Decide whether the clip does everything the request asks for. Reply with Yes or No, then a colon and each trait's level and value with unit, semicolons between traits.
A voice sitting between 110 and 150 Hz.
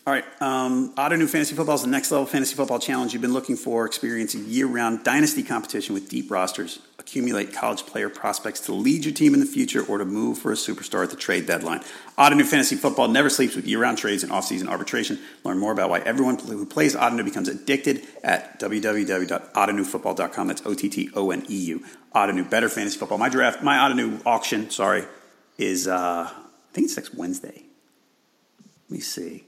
Yes: medium, 140 Hz